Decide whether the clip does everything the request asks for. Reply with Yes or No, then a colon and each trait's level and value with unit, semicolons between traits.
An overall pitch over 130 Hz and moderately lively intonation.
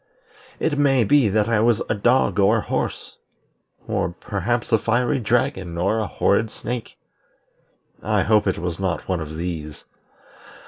No: low, 105 Hz; average, 4.2 semitones